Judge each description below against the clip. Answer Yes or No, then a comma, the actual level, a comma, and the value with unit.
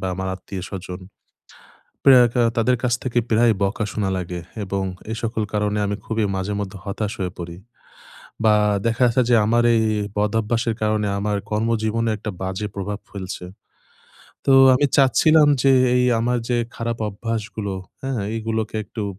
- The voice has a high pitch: No, low, 110 Hz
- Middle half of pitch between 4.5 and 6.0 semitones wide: No, average, 2.7 semitones